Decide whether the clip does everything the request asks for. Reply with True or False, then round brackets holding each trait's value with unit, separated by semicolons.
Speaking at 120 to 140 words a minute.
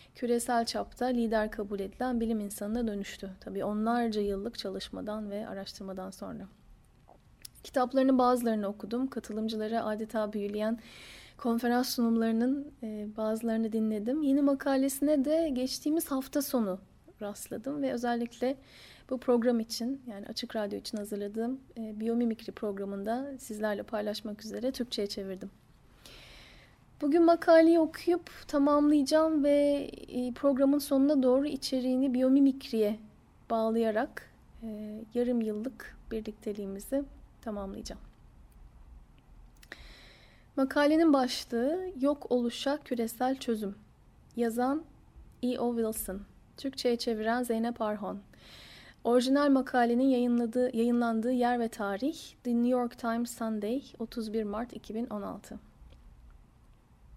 False (95 wpm)